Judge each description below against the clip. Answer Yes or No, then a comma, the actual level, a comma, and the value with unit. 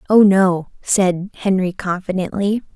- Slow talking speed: Yes, slow, 110 wpm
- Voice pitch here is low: No, high, 190 Hz